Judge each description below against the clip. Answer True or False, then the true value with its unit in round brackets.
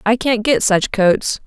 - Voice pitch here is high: True (220 Hz)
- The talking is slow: False (205 wpm)